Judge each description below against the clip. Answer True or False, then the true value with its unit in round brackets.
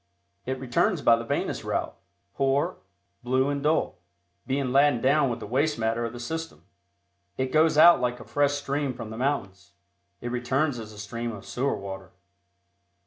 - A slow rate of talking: False (175 wpm)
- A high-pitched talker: False (130 Hz)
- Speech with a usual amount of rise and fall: True (3.6 semitones)